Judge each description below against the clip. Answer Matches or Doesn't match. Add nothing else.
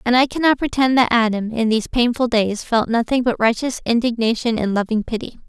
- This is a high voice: Matches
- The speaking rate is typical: Matches